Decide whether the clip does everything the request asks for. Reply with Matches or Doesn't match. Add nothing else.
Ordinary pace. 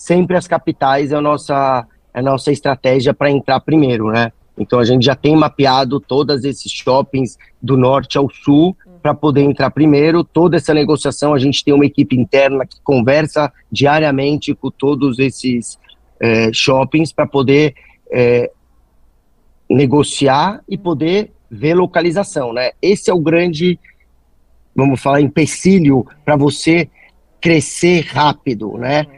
Matches